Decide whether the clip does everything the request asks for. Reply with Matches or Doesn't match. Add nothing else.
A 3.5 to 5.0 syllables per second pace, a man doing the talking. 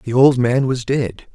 Matches